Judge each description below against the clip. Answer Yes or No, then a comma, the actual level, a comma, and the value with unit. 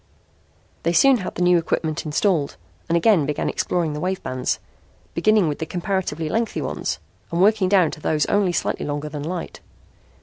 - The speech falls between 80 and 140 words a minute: No, average, 175 wpm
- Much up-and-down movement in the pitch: No, average, 3.9 semitones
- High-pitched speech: No, medium, 170 Hz